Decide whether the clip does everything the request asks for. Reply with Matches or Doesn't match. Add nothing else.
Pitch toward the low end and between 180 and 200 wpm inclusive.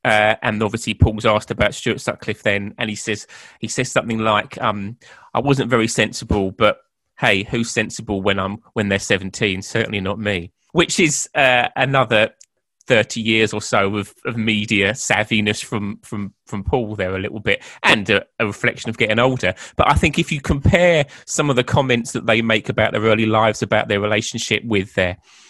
Matches